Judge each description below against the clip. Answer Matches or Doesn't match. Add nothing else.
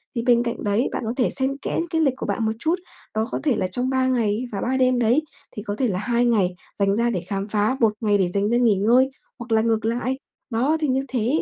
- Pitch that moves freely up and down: Doesn't match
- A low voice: Doesn't match